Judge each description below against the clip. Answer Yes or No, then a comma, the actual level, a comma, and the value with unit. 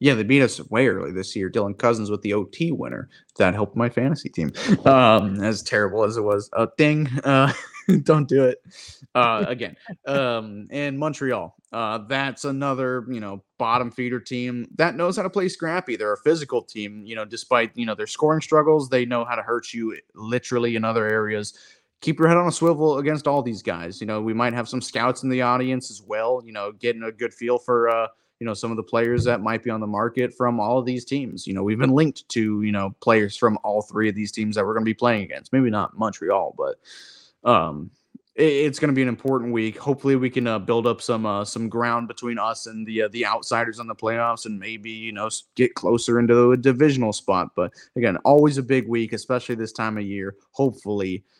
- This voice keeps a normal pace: No, fast, 230 wpm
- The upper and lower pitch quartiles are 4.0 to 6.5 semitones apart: No, average, 3.6 semitones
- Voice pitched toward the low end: Yes, low, 120 Hz